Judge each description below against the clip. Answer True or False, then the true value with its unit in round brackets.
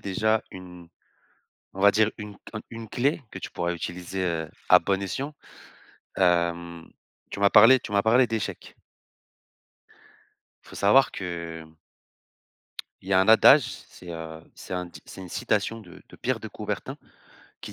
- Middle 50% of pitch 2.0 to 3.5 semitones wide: False (4.1 semitones)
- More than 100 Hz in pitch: False (95 Hz)